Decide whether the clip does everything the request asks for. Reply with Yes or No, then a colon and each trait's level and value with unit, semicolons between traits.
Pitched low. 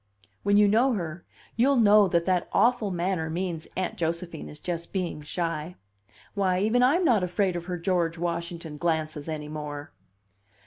No: medium, 175 Hz